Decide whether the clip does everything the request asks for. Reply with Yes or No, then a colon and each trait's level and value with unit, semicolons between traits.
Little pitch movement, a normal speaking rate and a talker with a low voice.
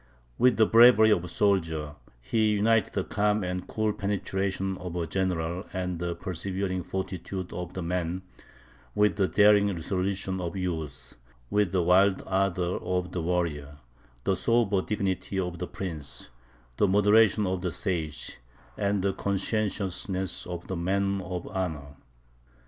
Yes: narrow, 2.2 semitones; average, 145 wpm; very low, 95 Hz